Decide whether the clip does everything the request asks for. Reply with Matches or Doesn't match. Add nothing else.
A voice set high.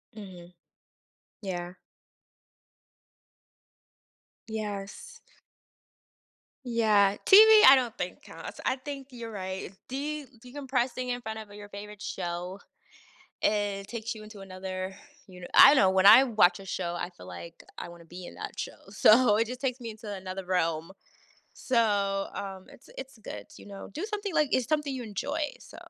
Matches